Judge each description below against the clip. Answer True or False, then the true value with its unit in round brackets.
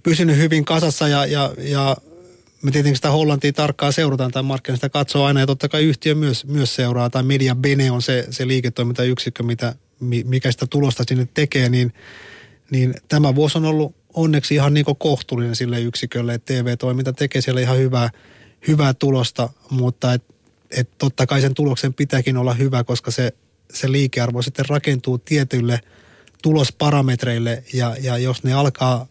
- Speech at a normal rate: False (165 wpm)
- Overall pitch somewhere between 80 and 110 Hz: False (130 Hz)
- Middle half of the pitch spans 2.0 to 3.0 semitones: True (2.7 semitones)